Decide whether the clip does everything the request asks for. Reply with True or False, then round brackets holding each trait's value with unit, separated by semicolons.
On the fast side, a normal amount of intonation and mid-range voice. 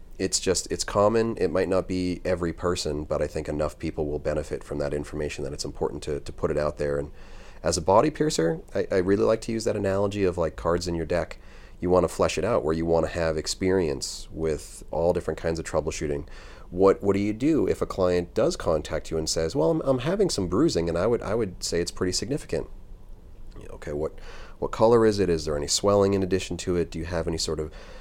False (240 wpm; 3.6 semitones; 90 Hz)